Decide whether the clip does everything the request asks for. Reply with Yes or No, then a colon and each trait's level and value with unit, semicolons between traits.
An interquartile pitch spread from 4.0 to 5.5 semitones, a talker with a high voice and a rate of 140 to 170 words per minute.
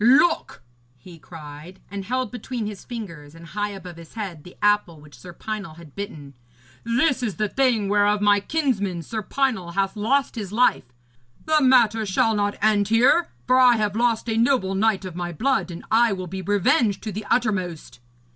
No: average, 4.6 semitones; high, 205 Hz; average, 185 wpm